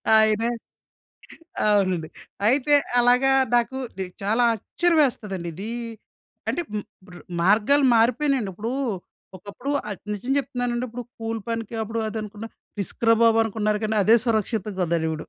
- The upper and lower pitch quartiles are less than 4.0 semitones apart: Yes, average, 3.0 semitones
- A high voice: Yes, high, 225 Hz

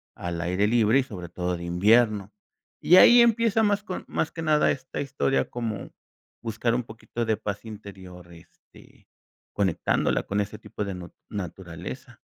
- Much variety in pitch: Yes, wide, 6.1 semitones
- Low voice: Yes, low, 105 Hz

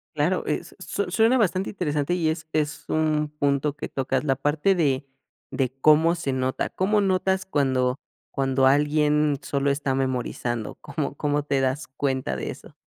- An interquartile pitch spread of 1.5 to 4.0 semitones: Yes, average, 2.9 semitones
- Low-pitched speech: No, medium, 145 Hz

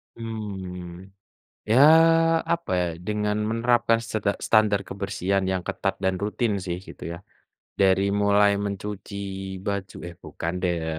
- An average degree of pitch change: No, narrow, 2.1 semitones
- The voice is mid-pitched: No, low, 100 Hz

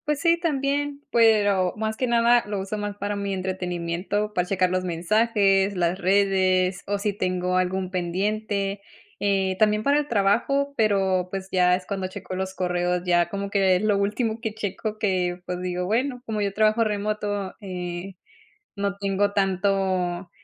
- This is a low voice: No, high, 195 Hz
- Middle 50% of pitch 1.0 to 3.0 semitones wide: Yes, narrow, 2.5 semitones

